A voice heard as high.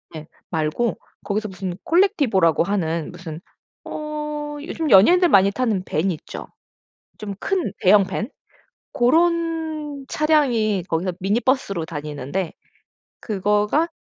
Yes: high, 210 Hz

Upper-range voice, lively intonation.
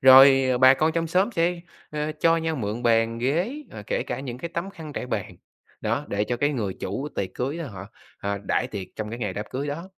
No: low, 135 Hz; wide, 6.2 semitones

